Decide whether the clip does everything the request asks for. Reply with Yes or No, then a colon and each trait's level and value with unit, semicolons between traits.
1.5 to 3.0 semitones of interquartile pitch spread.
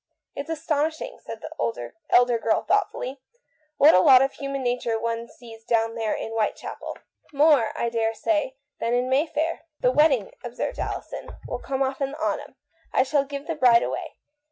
No: average, 4.4 semitones